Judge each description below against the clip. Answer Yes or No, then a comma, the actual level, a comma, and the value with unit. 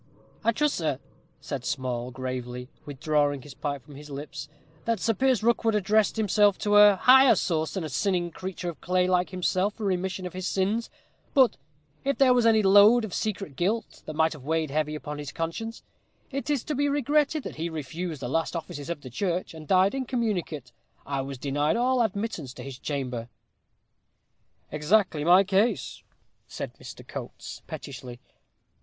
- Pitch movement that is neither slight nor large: No, wide, 6.9 semitones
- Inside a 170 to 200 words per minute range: Yes, average, 175 wpm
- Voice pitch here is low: No, medium, 180 Hz